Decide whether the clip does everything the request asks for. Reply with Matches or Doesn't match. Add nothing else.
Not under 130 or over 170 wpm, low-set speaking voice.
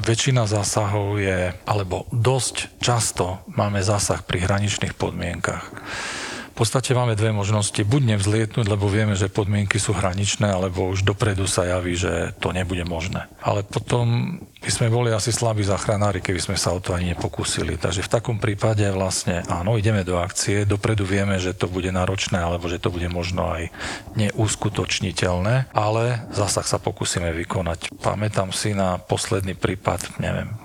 Matches